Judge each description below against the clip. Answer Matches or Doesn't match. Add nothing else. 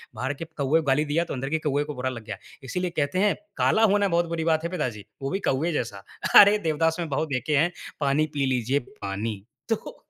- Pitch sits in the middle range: Matches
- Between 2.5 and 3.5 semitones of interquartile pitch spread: Doesn't match